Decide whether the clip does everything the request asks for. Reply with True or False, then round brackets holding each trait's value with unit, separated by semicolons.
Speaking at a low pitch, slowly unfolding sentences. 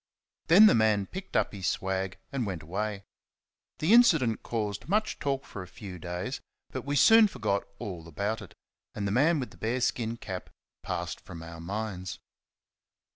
False (110 Hz; 175 wpm)